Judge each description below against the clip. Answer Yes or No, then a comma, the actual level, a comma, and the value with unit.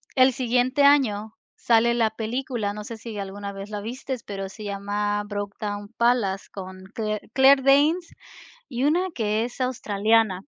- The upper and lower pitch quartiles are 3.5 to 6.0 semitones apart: Yes, average, 3.8 semitones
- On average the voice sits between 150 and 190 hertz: No, high, 220 Hz